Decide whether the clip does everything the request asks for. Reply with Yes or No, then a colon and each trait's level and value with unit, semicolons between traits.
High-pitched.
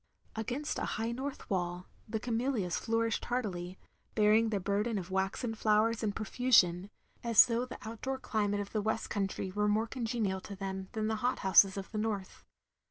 Yes: high, 215 Hz